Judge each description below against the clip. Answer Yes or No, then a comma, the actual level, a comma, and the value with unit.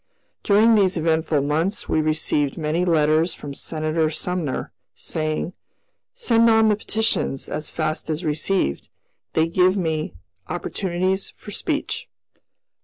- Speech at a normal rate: No, slow, 120 wpm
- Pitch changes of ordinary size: Yes, average, 3.5 semitones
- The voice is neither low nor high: Yes, medium, 165 Hz